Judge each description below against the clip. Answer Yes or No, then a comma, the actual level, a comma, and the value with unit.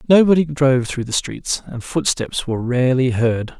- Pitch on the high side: No, low, 135 Hz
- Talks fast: No, average, 165 wpm